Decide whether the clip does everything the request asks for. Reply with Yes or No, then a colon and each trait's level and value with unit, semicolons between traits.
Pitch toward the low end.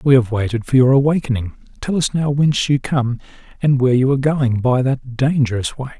Yes: low, 130 Hz